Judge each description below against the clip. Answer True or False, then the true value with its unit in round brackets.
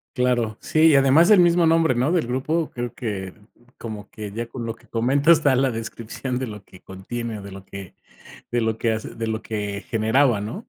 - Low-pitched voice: True (120 Hz)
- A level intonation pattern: False (4.0 semitones)